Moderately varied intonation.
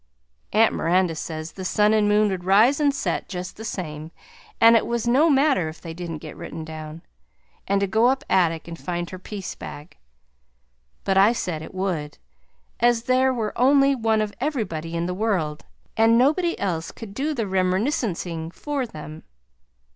No: wide, 6.0 semitones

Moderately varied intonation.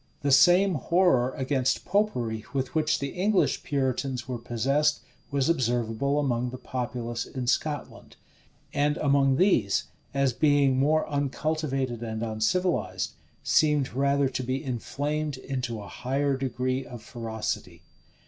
Yes: average, 3.1 semitones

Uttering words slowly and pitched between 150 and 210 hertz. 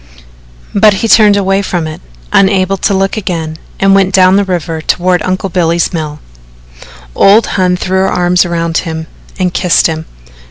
No: average, 165 wpm; medium, 185 Hz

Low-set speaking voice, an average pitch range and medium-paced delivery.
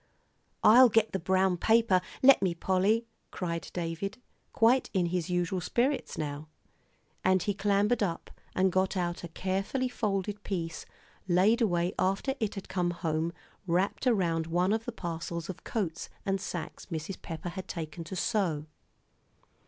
No: medium, 185 Hz; average, 3.3 semitones; average, 155 wpm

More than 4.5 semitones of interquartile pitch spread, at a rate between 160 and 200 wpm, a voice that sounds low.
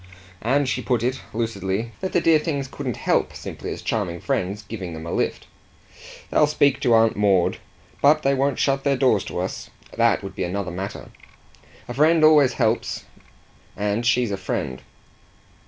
Yes: wide, 5.6 semitones; average, 170 wpm; low, 120 Hz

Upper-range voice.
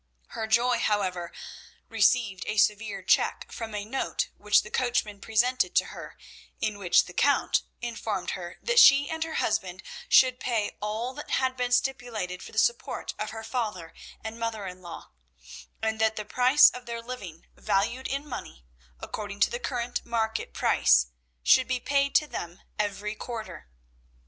Yes: high, 220 Hz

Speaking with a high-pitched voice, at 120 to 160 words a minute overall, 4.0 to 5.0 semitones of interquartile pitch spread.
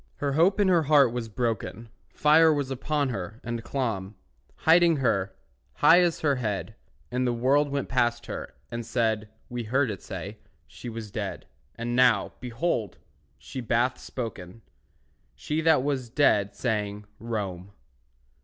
No: low, 120 Hz; average, 150 wpm; average, 4.4 semitones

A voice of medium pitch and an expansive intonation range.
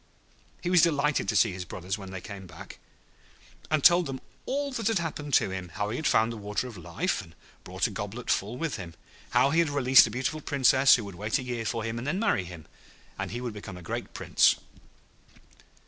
No: low, 120 Hz; wide, 6.8 semitones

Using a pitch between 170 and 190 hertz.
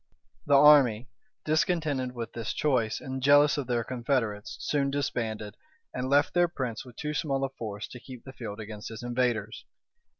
No: low, 130 Hz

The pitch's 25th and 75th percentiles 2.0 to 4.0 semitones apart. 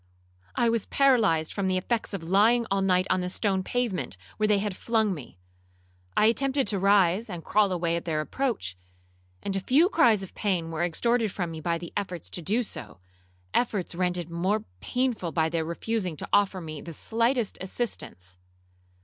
No: average, 4.9 semitones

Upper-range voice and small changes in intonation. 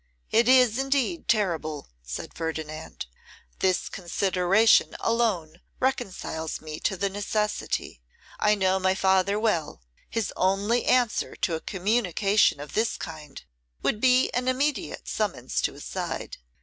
No: high, 200 Hz; average, 5.3 semitones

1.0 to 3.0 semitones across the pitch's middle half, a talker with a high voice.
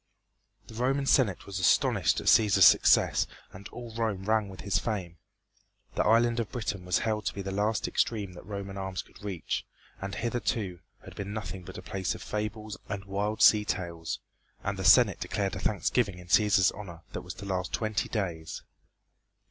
No: narrow, 2.4 semitones; low, 100 Hz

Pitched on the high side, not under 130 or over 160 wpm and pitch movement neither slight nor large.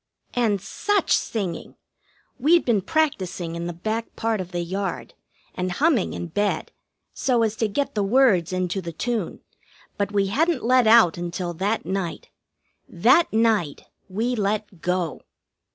Yes: high, 205 Hz; average, 150 wpm; average, 4.5 semitones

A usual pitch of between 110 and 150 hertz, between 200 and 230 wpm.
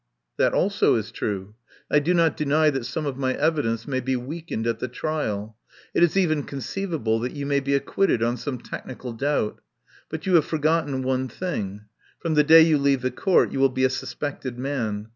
Yes: medium, 140 Hz; fast, 205 wpm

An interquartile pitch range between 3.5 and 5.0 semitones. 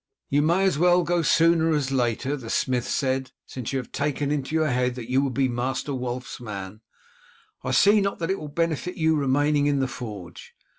Yes: average, 4.0 semitones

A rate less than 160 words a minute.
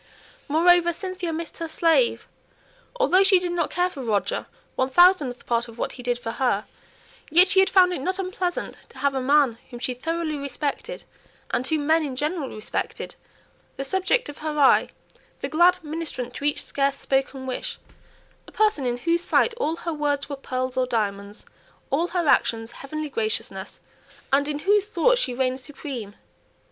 No: average, 175 wpm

